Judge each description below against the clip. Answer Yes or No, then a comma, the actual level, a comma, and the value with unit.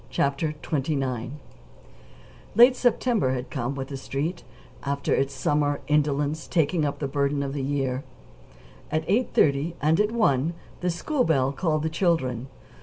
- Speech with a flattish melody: No, average, 3.3 semitones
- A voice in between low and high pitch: Yes, medium, 145 Hz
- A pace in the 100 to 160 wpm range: Yes, average, 150 wpm